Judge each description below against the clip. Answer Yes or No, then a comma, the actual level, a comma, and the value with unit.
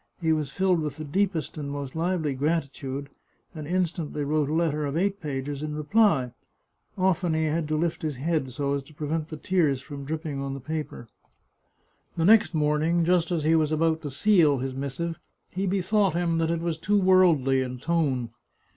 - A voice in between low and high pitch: Yes, medium, 155 Hz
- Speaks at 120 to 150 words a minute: No, average, 190 wpm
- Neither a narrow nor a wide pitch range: Yes, average, 3.1 semitones